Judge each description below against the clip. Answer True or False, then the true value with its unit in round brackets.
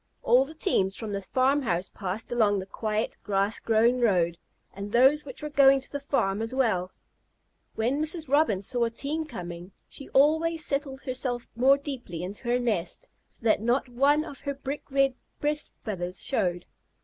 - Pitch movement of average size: False (5.7 semitones)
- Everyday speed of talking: True (180 wpm)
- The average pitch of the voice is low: False (245 Hz)